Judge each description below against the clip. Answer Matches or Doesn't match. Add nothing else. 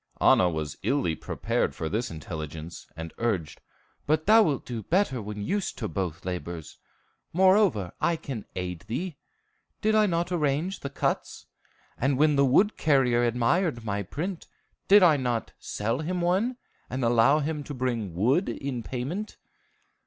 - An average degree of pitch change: Doesn't match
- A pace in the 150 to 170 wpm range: Matches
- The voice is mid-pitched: Doesn't match